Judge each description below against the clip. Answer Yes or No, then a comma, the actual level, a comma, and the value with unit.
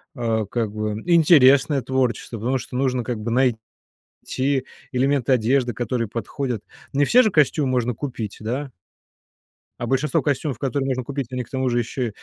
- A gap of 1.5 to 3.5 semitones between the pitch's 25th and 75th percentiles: Yes, average, 2.7 semitones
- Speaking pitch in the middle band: No, low, 130 Hz